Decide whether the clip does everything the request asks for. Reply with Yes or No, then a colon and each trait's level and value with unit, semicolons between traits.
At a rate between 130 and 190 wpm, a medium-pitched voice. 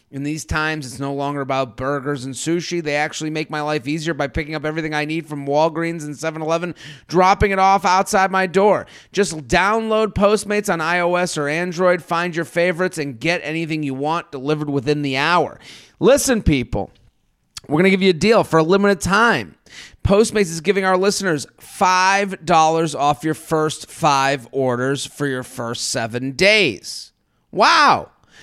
Yes: average, 175 wpm; medium, 160 Hz